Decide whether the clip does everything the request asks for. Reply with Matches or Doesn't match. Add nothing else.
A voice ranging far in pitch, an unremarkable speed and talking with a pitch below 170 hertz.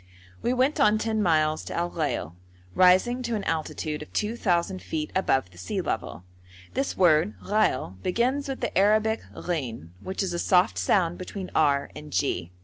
Doesn't match